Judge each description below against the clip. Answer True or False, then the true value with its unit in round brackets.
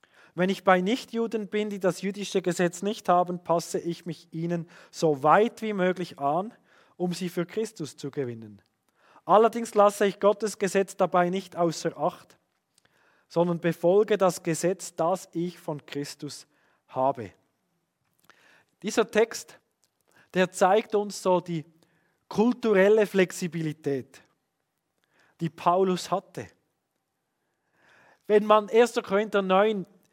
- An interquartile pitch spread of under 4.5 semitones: True (3.6 semitones)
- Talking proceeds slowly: True (120 wpm)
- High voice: False (180 Hz)